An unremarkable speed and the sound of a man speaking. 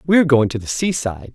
No: fast, 225 wpm; male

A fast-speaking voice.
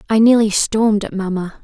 No: average, 185 wpm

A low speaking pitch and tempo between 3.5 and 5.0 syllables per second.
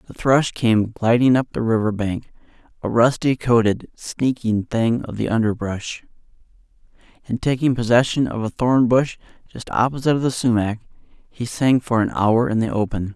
Yes: low, 115 Hz; 4.6 syllables/s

